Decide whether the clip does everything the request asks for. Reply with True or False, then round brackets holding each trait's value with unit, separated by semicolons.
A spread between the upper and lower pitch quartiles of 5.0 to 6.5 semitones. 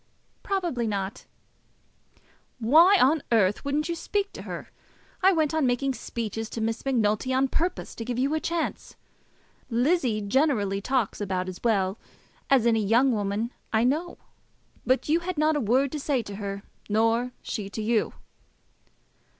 True (5.6 semitones)